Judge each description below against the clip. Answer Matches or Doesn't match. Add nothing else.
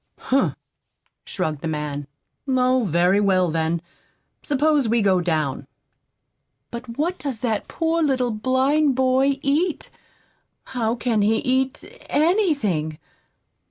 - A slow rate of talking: Matches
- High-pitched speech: Matches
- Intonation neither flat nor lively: Doesn't match